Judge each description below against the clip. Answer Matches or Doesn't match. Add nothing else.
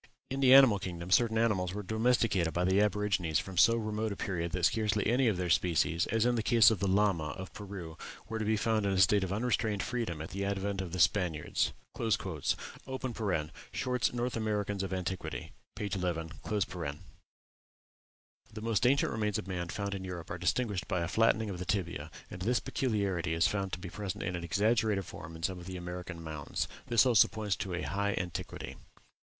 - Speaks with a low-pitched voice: Matches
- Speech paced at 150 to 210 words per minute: Matches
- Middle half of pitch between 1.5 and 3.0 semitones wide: Doesn't match